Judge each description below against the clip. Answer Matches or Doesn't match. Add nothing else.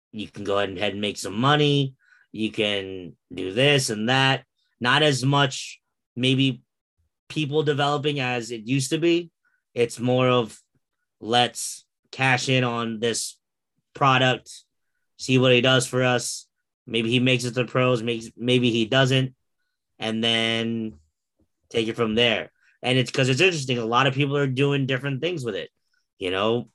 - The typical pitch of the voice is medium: Doesn't match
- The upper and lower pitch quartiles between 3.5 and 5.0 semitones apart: Doesn't match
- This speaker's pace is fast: Doesn't match